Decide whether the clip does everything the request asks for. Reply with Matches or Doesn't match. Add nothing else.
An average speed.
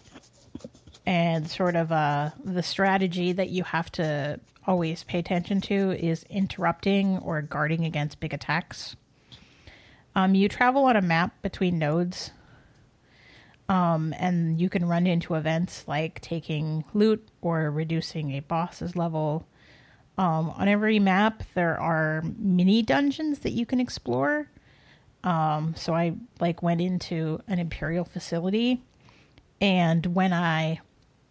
Doesn't match